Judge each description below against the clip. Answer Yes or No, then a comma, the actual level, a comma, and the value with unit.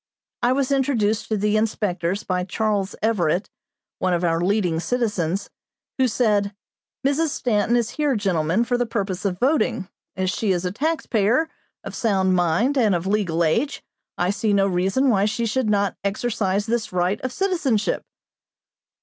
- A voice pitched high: Yes, high, 210 Hz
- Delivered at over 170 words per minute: No, average, 160 wpm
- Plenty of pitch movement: No, average, 4.3 semitones